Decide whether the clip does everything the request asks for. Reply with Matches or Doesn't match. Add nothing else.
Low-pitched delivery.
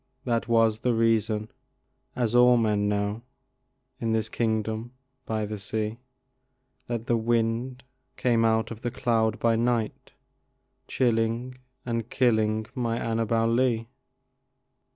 Matches